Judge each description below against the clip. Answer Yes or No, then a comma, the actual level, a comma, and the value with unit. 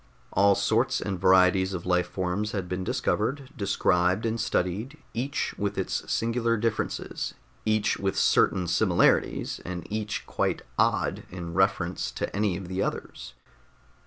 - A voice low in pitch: Yes, very low, 95 Hz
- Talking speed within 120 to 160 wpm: Yes, average, 140 wpm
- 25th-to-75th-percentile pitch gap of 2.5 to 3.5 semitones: Yes, average, 3.2 semitones